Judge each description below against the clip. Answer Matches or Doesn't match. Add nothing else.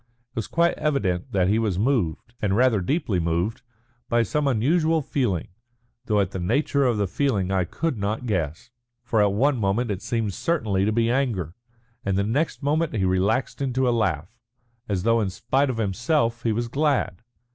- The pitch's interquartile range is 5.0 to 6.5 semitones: Matches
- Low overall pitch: Matches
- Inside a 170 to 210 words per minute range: Matches